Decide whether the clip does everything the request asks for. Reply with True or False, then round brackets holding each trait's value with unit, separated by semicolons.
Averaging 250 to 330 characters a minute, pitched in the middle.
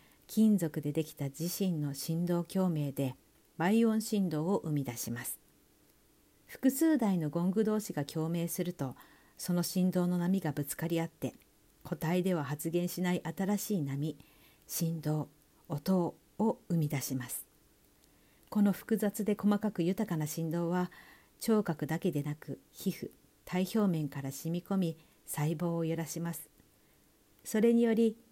True (260 characters per minute; 170 Hz)